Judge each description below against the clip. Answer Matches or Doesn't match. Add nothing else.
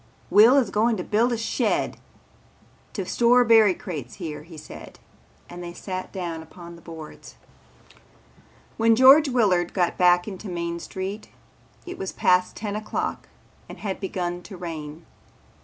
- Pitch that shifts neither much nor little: Matches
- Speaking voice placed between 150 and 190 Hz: Matches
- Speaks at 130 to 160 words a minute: Matches